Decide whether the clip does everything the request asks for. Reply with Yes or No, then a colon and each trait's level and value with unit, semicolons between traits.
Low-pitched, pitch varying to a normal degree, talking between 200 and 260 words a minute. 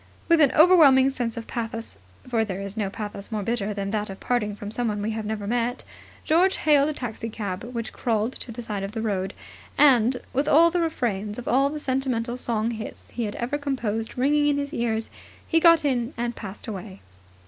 No: high, 235 Hz; average, 4.1 semitones; fast, 205 wpm